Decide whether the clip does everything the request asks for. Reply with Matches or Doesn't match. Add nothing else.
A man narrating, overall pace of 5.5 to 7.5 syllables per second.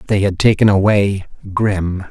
Doesn't match